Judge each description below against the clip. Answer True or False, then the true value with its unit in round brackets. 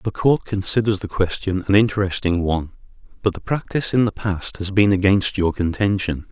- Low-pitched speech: True (100 Hz)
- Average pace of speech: True (180 wpm)